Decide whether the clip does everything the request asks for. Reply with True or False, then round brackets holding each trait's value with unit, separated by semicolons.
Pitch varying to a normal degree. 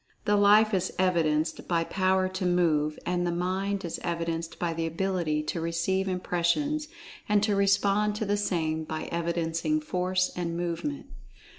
True (3.0 semitones)